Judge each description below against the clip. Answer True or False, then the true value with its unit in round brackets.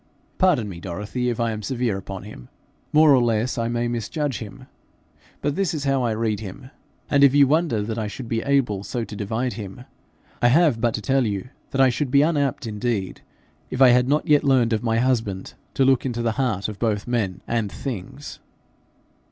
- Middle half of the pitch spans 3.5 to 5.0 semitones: True (3.9 semitones)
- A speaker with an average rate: False (210 wpm)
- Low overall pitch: True (120 Hz)